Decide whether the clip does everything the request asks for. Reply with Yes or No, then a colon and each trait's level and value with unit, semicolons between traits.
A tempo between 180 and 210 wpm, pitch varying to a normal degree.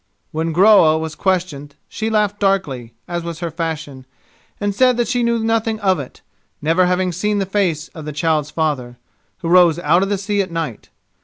Yes: average, 190 wpm; average, 4.6 semitones